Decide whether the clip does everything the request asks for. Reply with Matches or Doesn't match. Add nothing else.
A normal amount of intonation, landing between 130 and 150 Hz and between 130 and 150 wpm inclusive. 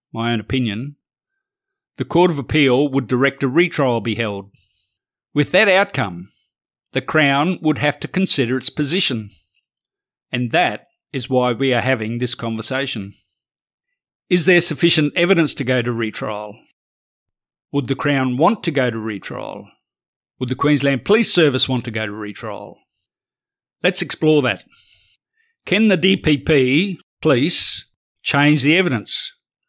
Doesn't match